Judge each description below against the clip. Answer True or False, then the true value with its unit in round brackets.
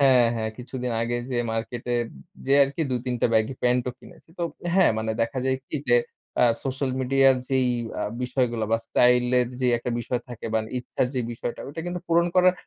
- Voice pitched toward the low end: True (125 Hz)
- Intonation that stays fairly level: True (2.1 semitones)